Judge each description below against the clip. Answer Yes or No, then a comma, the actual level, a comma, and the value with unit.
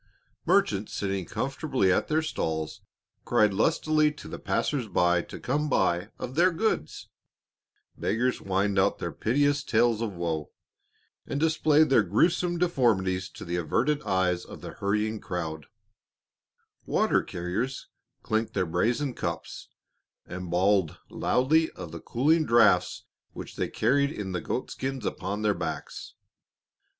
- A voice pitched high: No, low, 110 Hz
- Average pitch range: No, wide, 7.6 semitones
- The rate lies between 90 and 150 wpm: Yes, average, 140 wpm